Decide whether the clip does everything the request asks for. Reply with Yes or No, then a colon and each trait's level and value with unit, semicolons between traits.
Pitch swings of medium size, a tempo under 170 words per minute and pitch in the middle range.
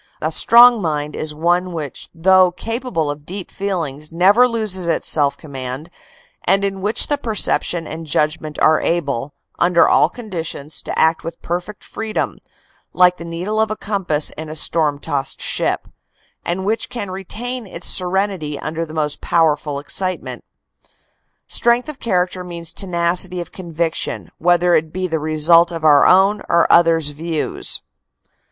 Yes: average, 3.6 semitones; average, 155 wpm; medium, 170 Hz